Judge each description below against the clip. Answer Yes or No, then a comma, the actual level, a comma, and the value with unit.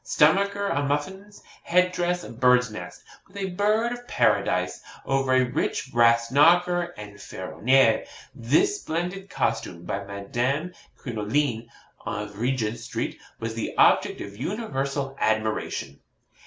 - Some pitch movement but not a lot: No, wide, 7.7 semitones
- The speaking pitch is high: No, low, 135 Hz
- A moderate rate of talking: No, slow, 130 wpm